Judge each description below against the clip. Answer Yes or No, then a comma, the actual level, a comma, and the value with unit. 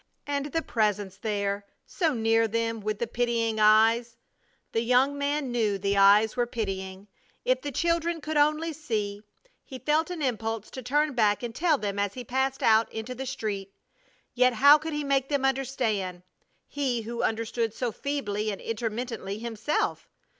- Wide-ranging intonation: No, average, 4.5 semitones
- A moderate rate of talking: Yes, average, 170 wpm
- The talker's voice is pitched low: No, high, 235 Hz